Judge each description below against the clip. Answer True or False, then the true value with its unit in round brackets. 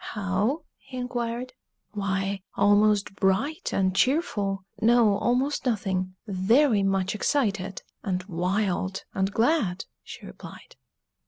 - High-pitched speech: True (205 Hz)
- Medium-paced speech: False (105 wpm)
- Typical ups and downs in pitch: True (4.1 semitones)